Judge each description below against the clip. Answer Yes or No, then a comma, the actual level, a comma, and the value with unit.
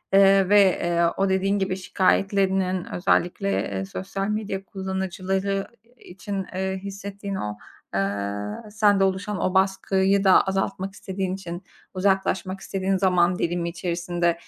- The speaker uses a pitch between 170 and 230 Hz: Yes, high, 190 Hz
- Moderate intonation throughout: No, narrow, 1.5 semitones